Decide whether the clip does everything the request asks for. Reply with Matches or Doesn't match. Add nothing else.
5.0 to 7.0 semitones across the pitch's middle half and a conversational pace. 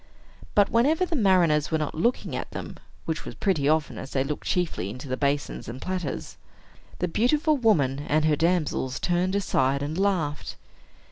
Matches